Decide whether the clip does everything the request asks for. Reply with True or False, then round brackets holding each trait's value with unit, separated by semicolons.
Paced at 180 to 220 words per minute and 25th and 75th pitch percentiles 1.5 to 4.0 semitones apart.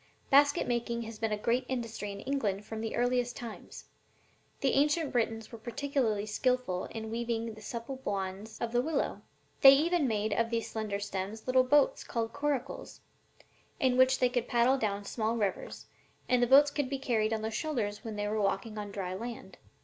True (190 wpm; 3.3 semitones)